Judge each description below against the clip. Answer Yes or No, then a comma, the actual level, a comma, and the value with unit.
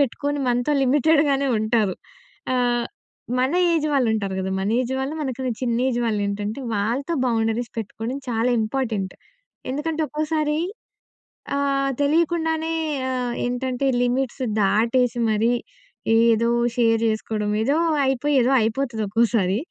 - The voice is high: Yes, high, 245 Hz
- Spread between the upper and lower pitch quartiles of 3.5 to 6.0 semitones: Yes, average, 3.8 semitones